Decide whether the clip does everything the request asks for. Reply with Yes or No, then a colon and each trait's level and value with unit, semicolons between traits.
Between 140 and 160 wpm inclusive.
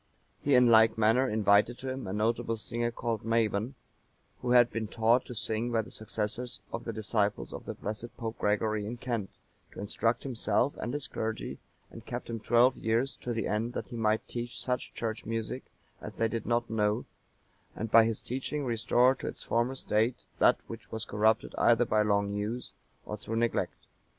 No: average, 190 wpm